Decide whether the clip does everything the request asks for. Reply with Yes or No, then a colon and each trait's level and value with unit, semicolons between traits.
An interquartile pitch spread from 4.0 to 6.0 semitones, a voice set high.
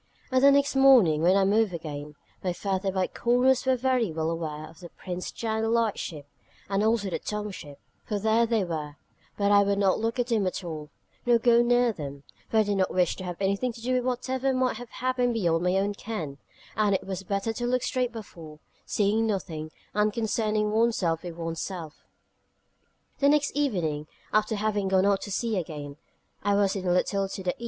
Yes: average, 4.7 semitones; high, 200 Hz